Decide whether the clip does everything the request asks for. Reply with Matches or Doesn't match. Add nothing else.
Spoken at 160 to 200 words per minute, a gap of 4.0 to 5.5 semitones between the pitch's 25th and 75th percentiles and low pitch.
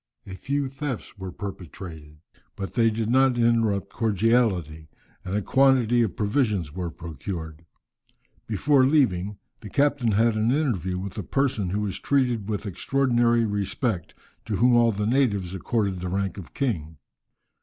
Doesn't match